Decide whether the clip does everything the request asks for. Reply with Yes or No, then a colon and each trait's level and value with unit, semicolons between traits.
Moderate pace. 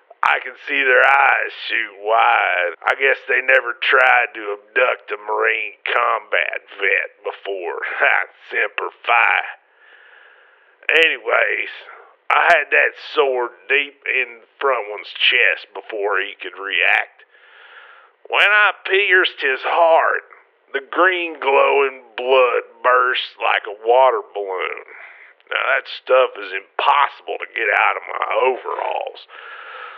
No: slow, 120 wpm